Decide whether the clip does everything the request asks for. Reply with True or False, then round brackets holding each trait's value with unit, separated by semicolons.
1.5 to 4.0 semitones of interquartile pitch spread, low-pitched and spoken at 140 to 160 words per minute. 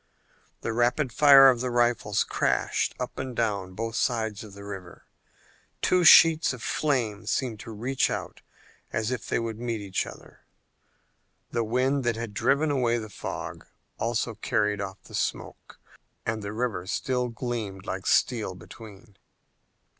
True (3.3 semitones; 115 Hz; 155 wpm)